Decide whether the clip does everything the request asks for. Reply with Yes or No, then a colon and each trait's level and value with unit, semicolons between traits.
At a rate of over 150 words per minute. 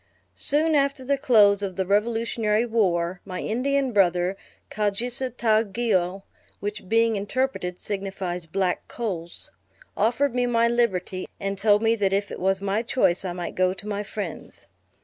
Yes: average, 165 wpm